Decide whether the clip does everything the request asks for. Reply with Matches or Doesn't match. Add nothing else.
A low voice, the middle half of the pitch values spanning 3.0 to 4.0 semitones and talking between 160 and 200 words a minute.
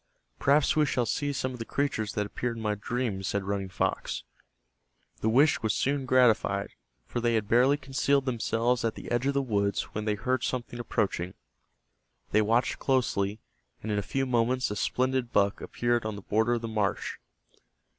Matches